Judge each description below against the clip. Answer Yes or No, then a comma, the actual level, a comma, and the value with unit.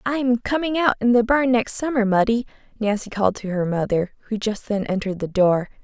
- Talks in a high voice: Yes, high, 220 Hz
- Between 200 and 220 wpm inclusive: Yes, fast, 205 wpm